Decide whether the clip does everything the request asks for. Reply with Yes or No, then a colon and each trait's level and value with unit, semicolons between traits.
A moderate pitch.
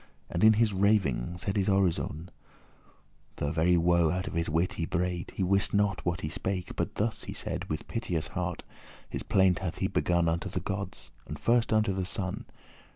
No: very low, 90 Hz